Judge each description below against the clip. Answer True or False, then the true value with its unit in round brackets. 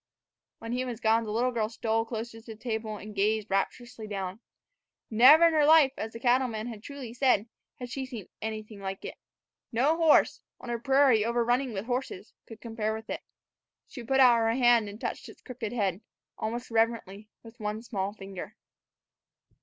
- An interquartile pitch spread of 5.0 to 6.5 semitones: False (2.5 semitones)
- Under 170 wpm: False (180 wpm)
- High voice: True (230 Hz)